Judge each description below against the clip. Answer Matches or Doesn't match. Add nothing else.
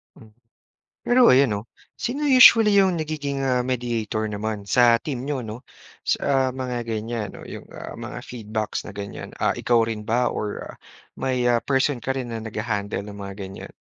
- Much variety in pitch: Doesn't match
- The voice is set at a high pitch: Doesn't match